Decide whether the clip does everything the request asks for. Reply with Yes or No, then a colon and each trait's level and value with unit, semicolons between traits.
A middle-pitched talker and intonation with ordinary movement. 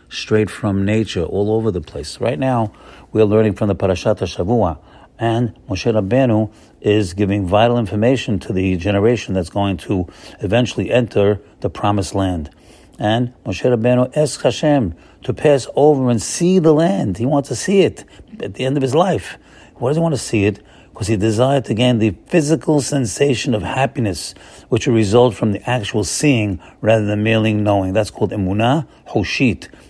No: low, 110 Hz; average, 3.8 semitones